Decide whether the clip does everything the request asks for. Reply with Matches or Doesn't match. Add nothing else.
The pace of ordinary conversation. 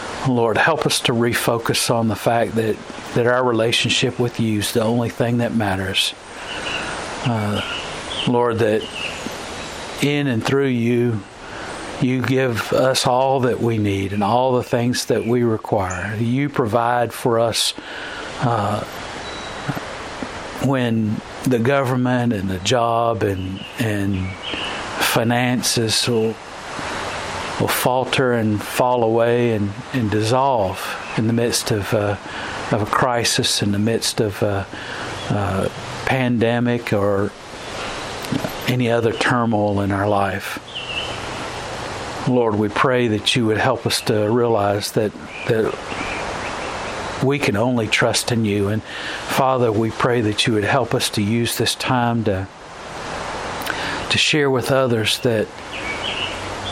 Doesn't match